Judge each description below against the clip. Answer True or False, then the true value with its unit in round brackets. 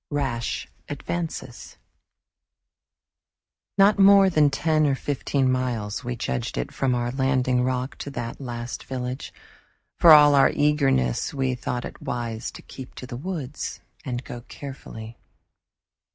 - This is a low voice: True (130 Hz)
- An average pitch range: True (3.1 semitones)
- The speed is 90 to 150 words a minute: True (135 wpm)